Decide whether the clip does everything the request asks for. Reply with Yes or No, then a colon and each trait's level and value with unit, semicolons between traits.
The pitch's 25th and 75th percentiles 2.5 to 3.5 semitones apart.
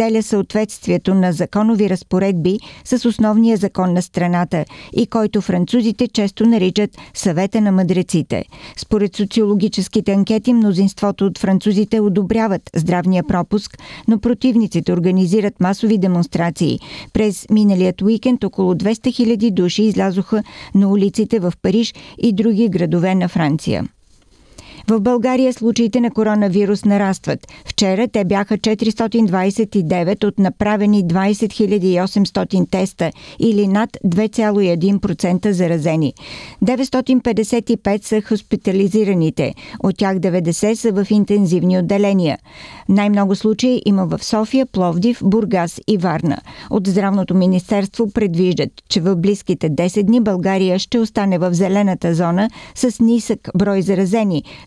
Yes: average, 3.0 semitones